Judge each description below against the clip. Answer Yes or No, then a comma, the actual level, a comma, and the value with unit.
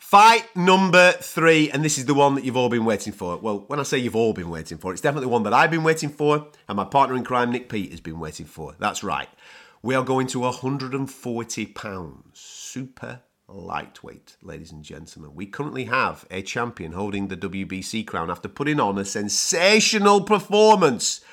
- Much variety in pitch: Yes, wide, 7.1 semitones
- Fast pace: No, average, 195 wpm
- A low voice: Yes, low, 125 Hz